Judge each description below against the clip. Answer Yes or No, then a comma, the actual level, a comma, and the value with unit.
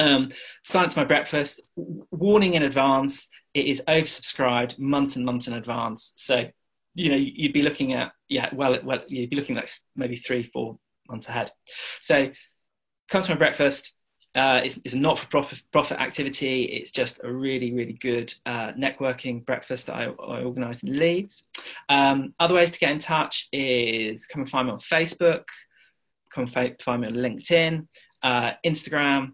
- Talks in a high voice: No, low, 135 Hz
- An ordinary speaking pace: Yes, average, 170 wpm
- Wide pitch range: No, average, 3.7 semitones